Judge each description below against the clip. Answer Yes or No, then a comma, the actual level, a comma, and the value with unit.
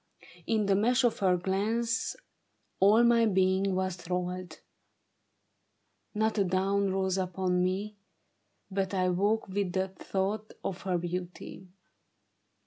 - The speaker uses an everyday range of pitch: No, narrow, 2.2 semitones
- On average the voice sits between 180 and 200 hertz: Yes, high, 190 Hz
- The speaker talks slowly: Yes, slow, 125 wpm